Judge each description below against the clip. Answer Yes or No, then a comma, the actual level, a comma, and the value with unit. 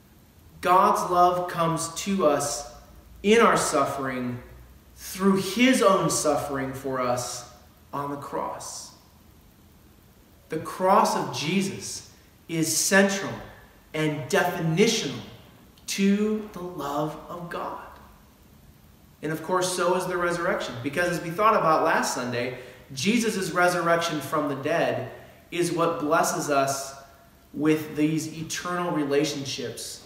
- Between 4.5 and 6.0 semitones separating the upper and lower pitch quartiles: Yes, average, 5.1 semitones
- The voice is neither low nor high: Yes, medium, 155 Hz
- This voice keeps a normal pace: No, slow, 115 wpm